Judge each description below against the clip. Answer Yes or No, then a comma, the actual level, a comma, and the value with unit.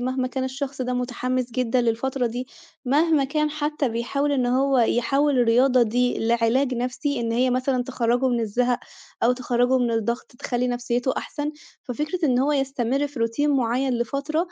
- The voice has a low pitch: No, very high, 255 Hz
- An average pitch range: No, narrow, 2.3 semitones